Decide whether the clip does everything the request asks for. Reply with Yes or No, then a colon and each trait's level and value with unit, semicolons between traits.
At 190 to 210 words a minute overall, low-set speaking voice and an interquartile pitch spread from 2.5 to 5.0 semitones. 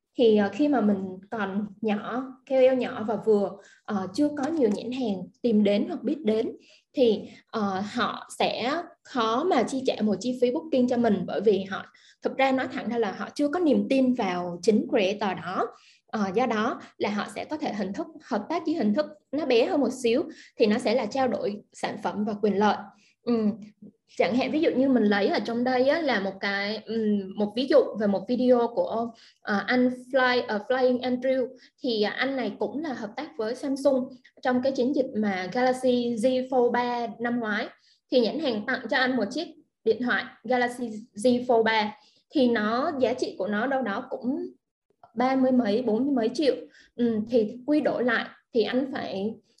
No: average, 205 wpm; high, 240 Hz; average, 3.4 semitones